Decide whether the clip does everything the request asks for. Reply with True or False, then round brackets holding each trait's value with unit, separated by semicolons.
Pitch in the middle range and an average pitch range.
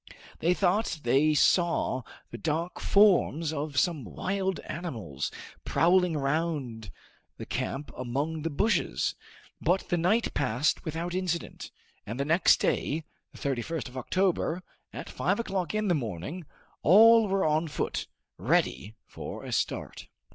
True (160 Hz; 4.7 semitones)